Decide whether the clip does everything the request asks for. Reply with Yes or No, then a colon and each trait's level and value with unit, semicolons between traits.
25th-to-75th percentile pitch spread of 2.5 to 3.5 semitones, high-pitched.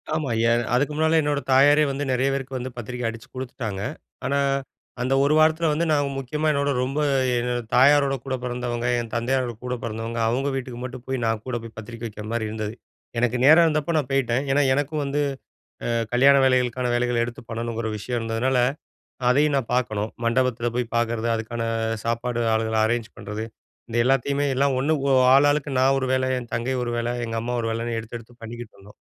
No: average, 2.8 semitones; low, 125 Hz